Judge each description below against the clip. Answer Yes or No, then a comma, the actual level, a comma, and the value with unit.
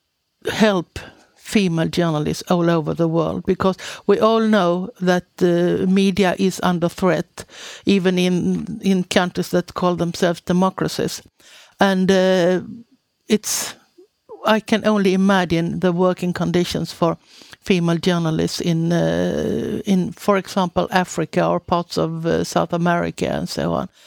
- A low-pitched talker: No, medium, 180 Hz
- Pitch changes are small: Yes, narrow, 2.2 semitones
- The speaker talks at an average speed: No, slow, 130 wpm